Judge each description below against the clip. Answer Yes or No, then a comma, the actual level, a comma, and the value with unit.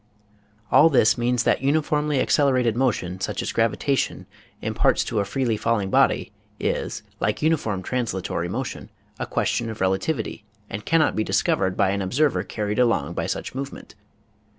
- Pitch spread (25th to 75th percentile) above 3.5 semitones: Yes, average, 5.3 semitones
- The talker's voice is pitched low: Yes, low, 115 Hz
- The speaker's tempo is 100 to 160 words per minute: Yes, average, 155 wpm